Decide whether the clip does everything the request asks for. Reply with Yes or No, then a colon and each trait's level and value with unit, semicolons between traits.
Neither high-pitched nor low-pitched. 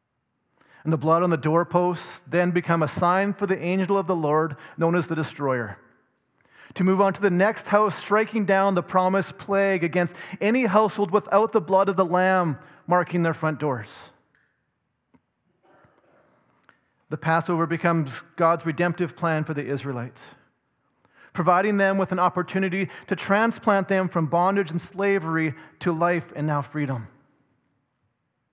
Yes: medium, 175 Hz